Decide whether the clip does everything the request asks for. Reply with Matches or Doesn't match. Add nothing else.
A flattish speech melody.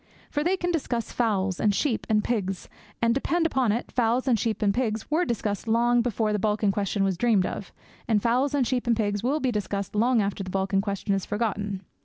Doesn't match